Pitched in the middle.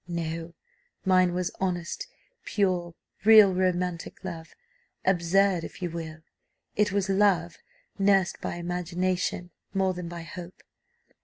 Yes: medium, 180 Hz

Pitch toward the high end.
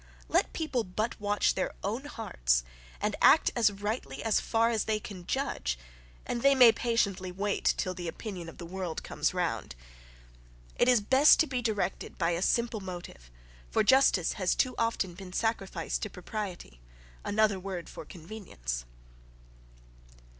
Yes: high, 200 Hz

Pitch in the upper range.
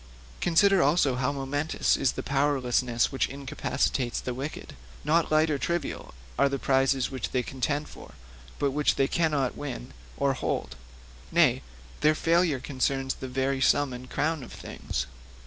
No: low, 135 Hz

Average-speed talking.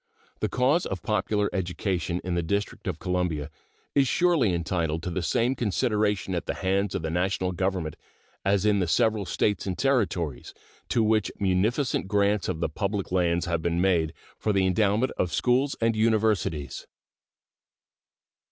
Yes: average, 160 wpm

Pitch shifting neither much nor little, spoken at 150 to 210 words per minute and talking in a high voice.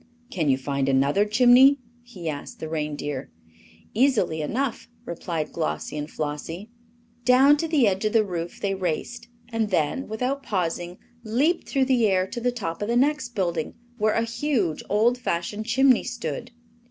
No: wide, 7.0 semitones; average, 165 wpm; high, 210 Hz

